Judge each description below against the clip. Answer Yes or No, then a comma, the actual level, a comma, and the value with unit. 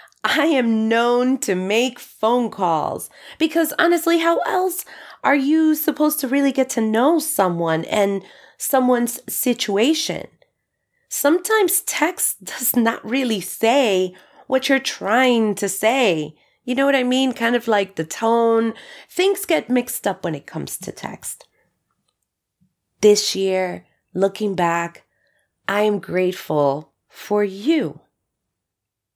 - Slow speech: Yes, slow, 130 wpm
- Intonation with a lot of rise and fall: Yes, wide, 5.9 semitones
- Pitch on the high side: Yes, high, 230 Hz